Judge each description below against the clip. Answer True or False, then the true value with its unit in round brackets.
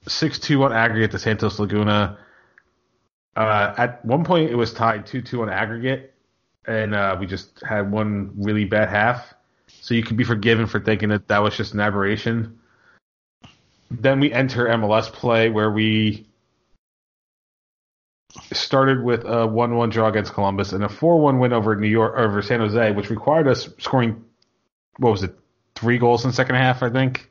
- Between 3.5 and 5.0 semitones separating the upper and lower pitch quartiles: False (2.4 semitones)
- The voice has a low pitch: True (115 Hz)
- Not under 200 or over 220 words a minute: False (170 wpm)